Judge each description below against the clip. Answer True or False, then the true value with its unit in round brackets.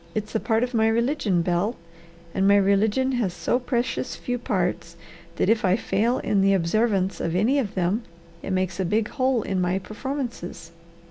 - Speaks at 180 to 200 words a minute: True (185 wpm)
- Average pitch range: True (4.3 semitones)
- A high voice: True (210 Hz)